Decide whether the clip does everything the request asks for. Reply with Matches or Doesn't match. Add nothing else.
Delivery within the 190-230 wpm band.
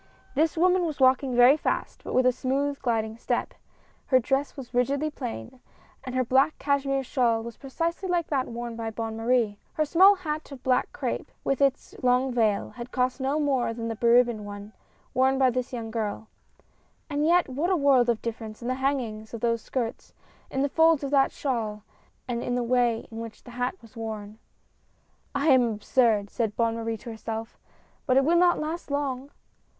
Matches